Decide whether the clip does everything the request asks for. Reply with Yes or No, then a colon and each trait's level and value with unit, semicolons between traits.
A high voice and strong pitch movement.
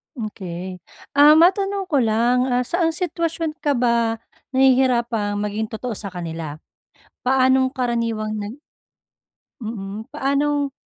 No: high, 245 Hz; average, 4.8 semitones